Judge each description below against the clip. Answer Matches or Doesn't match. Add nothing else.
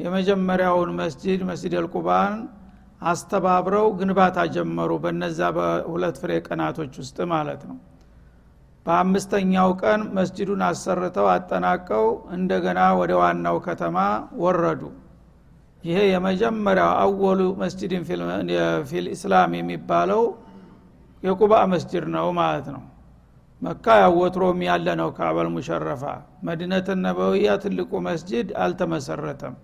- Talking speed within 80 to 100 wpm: Matches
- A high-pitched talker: Doesn't match